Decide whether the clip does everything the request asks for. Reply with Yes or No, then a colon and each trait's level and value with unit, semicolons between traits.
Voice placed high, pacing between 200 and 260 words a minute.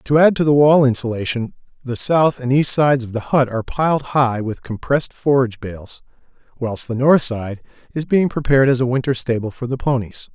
No: low, 130 Hz; fast, 205 wpm